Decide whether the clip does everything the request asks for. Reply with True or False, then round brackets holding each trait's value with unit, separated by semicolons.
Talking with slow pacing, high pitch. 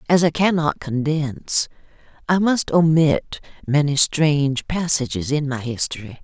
False (125 wpm; 145 Hz)